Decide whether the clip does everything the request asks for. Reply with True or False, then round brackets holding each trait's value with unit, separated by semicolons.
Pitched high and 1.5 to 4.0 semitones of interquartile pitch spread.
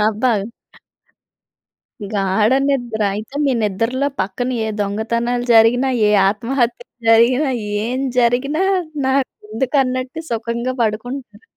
True (240 Hz; 2.8 semitones)